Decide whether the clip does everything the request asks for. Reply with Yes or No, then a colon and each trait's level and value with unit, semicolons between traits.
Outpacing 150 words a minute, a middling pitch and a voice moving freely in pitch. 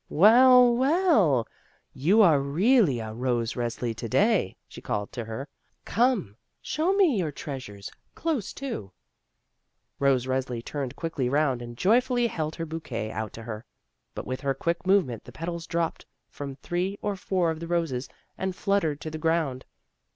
Yes: average, 160 wpm; medium, 155 Hz; wide, 7.9 semitones